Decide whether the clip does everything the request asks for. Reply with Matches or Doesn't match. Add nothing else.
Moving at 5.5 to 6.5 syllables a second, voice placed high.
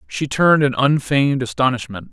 Doesn't match